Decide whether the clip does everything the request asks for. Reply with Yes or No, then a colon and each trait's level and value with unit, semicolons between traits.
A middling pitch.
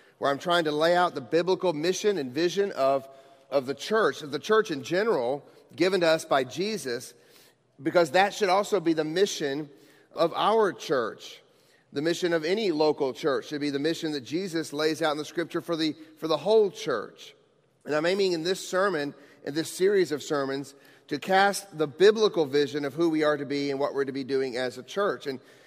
Yes: medium, 160 Hz